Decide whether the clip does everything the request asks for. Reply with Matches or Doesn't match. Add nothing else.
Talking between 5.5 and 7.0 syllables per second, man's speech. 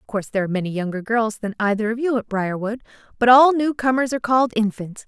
Doesn't match